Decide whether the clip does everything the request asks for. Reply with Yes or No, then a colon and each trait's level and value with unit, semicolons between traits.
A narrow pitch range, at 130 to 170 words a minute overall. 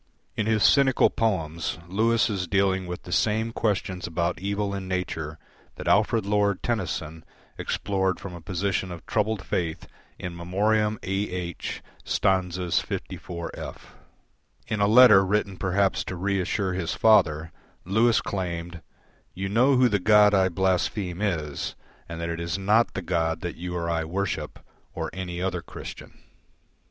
No: average, 3.0 semitones; average, 150 wpm